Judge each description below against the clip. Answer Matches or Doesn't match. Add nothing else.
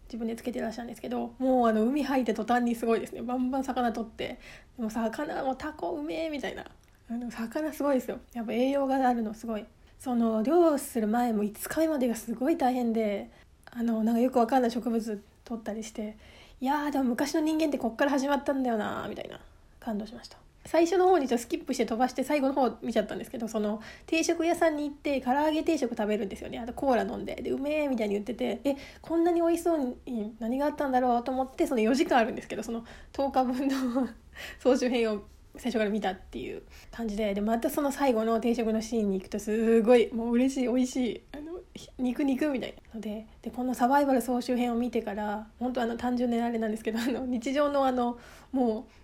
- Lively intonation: Doesn't match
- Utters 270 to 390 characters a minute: Doesn't match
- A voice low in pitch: Doesn't match